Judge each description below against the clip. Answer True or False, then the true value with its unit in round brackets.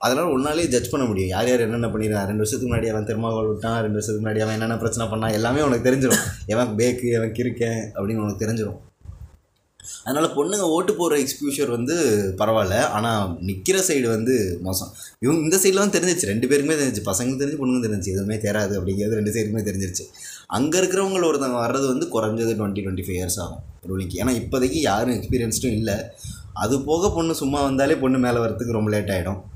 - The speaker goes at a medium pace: False (185 wpm)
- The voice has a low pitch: True (115 Hz)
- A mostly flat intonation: False (3.9 semitones)